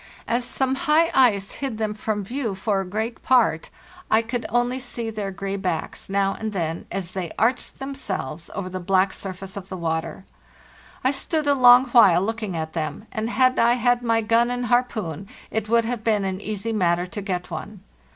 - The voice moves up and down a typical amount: Yes, average, 4.3 semitones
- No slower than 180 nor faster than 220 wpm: Yes, average, 195 wpm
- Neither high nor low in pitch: No, high, 215 Hz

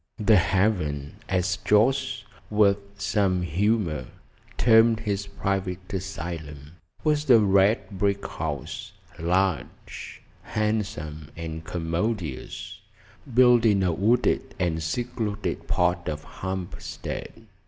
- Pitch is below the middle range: Yes, very low, 95 Hz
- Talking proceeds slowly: Yes, slow, 100 wpm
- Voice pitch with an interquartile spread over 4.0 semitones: Yes, average, 4.4 semitones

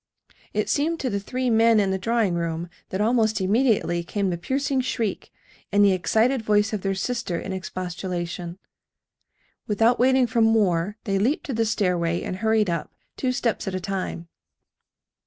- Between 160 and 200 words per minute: Yes, average, 170 wpm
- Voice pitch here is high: Yes, high, 205 Hz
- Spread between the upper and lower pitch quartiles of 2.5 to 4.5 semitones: Yes, average, 4.0 semitones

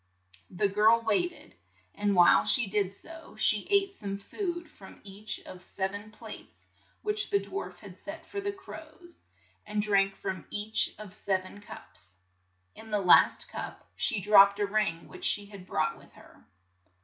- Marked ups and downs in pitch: Yes, wide, 7.9 semitones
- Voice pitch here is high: Yes, high, 210 Hz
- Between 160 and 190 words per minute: Yes, average, 175 wpm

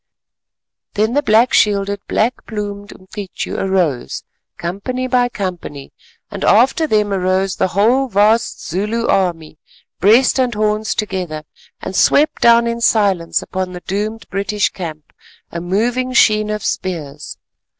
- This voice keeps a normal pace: No, slow, 130 wpm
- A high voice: Yes, high, 205 Hz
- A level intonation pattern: No, average, 3.8 semitones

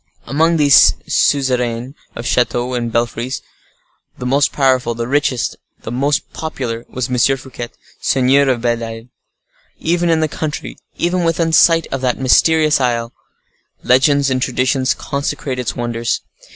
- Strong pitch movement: No, average, 3.1 semitones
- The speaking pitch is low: Yes, low, 130 Hz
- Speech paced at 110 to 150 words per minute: Yes, average, 140 wpm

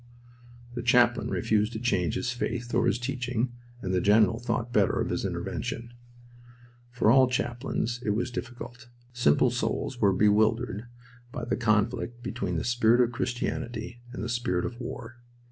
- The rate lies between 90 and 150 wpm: No, average, 160 wpm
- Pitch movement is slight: Yes, narrow, 1.9 semitones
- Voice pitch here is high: No, low, 120 Hz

